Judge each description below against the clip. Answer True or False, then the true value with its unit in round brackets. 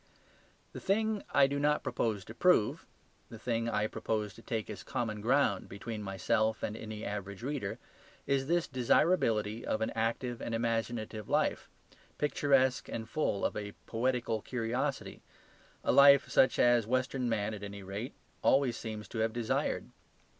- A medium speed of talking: True (155 wpm)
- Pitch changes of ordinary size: True (3.3 semitones)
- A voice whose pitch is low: True (115 Hz)